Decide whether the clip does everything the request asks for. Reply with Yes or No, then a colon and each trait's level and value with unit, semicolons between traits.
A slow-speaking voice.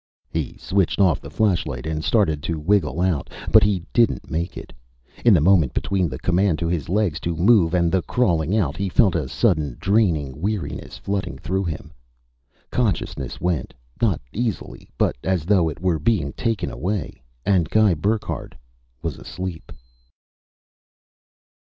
No: average, 155 wpm